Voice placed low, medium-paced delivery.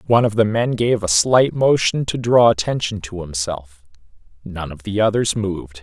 Yes: low, 100 Hz; average, 185 wpm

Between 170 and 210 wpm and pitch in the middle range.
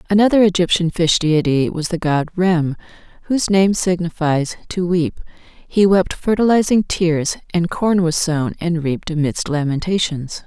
No: average, 145 wpm; medium, 170 Hz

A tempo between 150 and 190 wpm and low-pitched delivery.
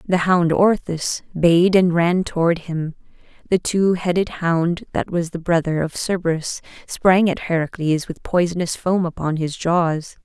No: average, 160 wpm; medium, 170 Hz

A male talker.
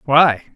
Yes: male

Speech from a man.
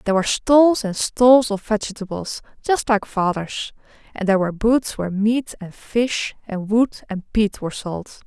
No: female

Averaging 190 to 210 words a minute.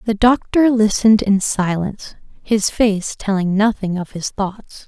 No: average, 150 wpm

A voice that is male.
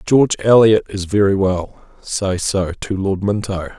Yes: male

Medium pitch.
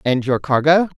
Yes: medium, 150 Hz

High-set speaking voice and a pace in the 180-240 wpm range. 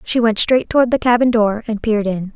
No: high, 225 Hz; fast, 255 wpm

